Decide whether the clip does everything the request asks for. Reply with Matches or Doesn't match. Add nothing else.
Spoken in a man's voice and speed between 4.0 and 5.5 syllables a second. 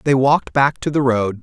Matches